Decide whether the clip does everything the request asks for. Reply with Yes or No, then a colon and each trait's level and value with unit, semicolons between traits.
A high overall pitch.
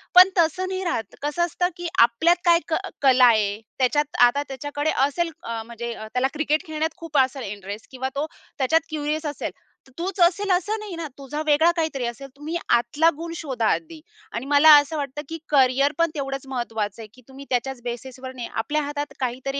Yes: very high, 285 Hz